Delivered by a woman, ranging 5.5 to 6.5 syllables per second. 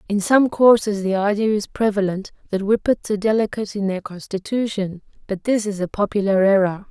Yes: female; 5.6 syllables/s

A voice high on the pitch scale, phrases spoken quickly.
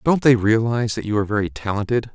No: low, 110 Hz; fast, 225 wpm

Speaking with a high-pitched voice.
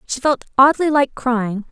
Yes: very high, 260 Hz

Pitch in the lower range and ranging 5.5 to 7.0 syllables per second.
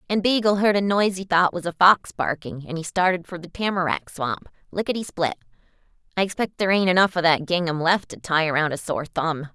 No: medium, 175 Hz; 5.8 syllables/s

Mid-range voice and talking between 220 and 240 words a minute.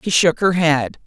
Yes: medium, 170 Hz; fast, 225 wpm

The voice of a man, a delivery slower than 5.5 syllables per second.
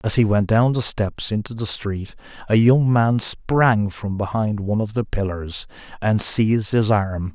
Yes: male; 4.3 syllables/s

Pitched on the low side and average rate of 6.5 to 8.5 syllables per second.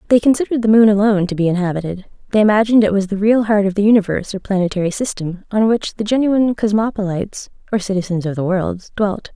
No: high, 205 Hz; 6.9 syllables/s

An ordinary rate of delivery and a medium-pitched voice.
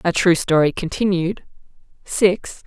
No: slow, 115 wpm; medium, 180 Hz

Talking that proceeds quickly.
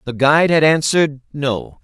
No: average, 165 wpm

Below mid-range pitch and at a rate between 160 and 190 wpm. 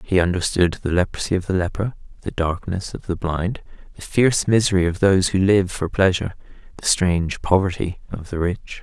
Yes: very low, 90 Hz; average, 185 wpm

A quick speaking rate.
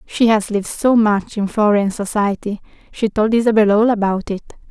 No: average, 180 wpm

